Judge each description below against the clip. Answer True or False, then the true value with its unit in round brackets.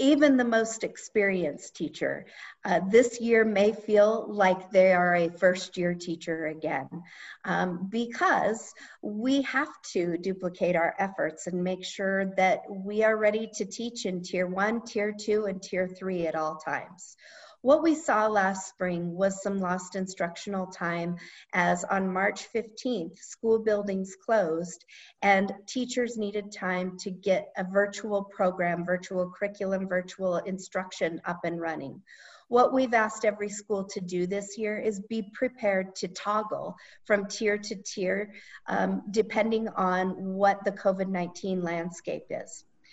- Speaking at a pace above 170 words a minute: False (150 wpm)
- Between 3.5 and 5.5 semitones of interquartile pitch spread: False (2.8 semitones)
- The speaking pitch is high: True (195 Hz)